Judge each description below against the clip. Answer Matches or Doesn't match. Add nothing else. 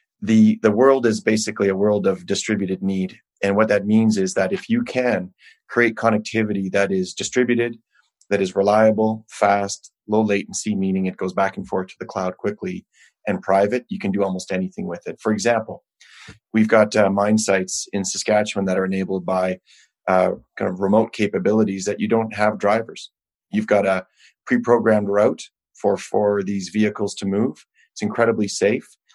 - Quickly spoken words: Doesn't match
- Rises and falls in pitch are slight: Matches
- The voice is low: Matches